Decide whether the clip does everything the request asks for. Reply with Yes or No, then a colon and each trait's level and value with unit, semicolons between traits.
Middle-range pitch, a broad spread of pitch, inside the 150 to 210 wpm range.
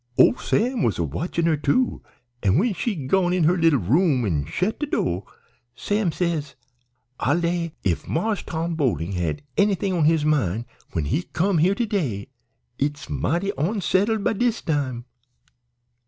Yes: medium, 165 Hz; wide, 7.0 semitones; average, 165 wpm